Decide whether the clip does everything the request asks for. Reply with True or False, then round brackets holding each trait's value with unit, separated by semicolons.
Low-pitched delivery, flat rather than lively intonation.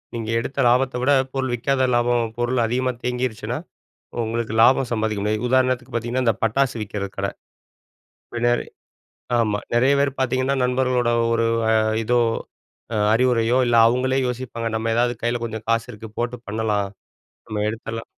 True (120 Hz; 2.2 semitones)